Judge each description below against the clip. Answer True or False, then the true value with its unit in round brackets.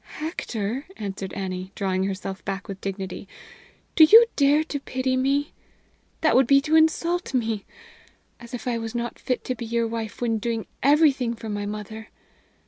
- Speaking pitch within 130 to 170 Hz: False (235 Hz)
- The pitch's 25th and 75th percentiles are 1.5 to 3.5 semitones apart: False (5.2 semitones)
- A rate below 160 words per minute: False (170 wpm)